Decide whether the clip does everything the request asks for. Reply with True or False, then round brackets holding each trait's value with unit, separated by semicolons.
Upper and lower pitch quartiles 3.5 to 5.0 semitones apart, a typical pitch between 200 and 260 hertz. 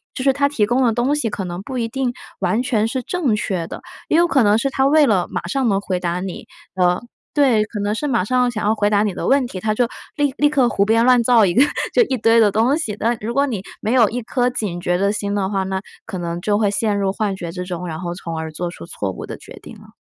True (4.7 semitones; 215 Hz)